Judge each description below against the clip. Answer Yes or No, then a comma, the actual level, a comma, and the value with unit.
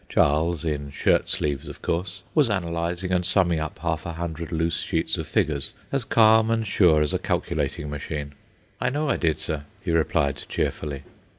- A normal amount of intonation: Yes, average, 3.4 semitones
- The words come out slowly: No, average, 180 wpm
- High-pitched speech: No, very low, 85 Hz